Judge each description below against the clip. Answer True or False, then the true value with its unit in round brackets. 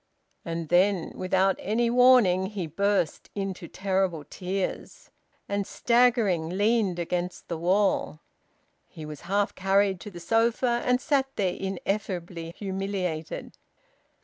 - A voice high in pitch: True (195 Hz)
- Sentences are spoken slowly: True (120 wpm)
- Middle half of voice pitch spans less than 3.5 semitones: True (2.9 semitones)